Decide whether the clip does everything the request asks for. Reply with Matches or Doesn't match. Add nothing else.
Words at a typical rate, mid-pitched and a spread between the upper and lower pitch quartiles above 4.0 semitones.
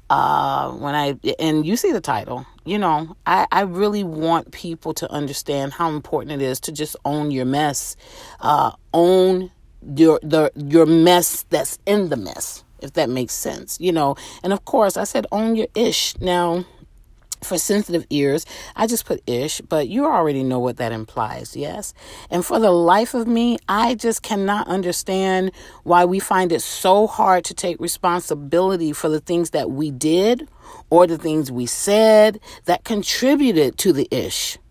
Matches